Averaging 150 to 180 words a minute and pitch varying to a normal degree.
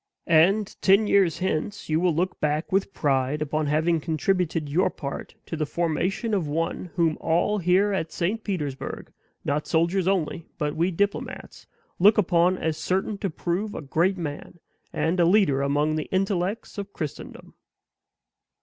Yes: average, 160 wpm; average, 3.8 semitones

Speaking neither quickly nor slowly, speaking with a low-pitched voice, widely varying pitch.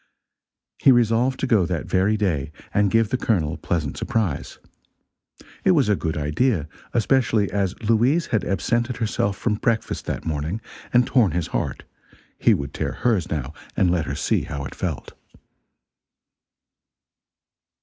Yes: average, 150 wpm; low, 105 Hz; wide, 6.3 semitones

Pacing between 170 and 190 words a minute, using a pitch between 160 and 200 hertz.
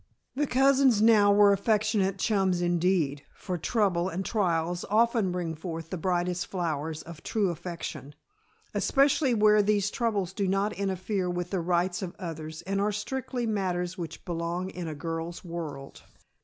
No: average, 155 wpm; medium, 185 Hz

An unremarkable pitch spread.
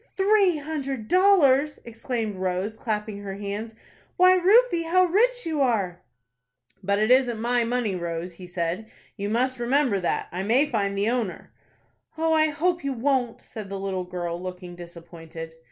No: wide, 7.5 semitones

